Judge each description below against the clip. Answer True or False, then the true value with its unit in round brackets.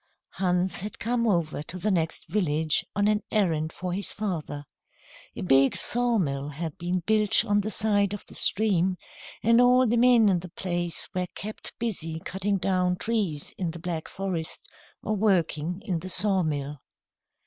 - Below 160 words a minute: False (165 wpm)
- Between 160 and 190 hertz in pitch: True (185 Hz)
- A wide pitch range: False (4.2 semitones)